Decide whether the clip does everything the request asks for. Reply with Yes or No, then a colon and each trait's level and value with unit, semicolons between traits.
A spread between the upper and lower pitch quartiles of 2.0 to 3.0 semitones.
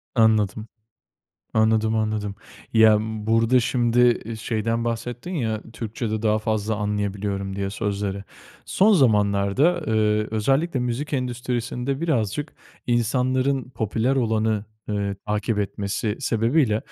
Yes: narrow, 2.6 semitones